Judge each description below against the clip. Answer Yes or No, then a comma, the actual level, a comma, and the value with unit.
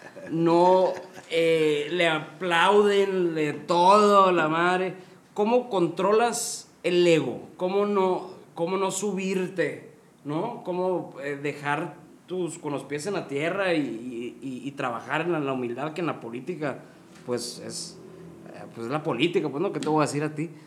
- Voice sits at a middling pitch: Yes, medium, 170 Hz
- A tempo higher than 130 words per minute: Yes, average, 165 wpm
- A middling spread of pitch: Yes, average, 3.4 semitones